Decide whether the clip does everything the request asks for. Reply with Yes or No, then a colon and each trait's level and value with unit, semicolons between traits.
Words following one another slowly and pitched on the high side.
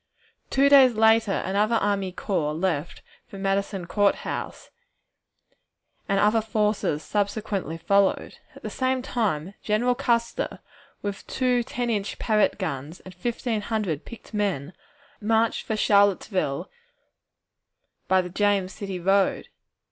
Yes: slow, 125 wpm; high, 205 Hz